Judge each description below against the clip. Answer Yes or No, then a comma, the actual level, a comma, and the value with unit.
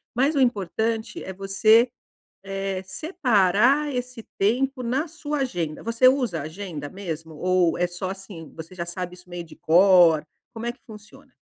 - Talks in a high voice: Yes, high, 195 Hz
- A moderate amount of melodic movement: No, wide, 5.7 semitones